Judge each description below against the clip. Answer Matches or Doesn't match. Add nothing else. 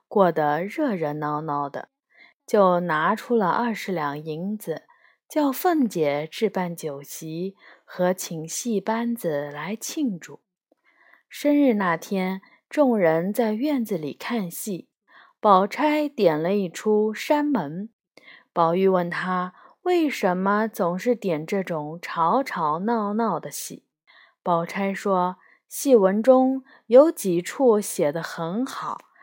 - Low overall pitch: Doesn't match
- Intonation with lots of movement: Matches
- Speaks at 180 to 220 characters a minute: Doesn't match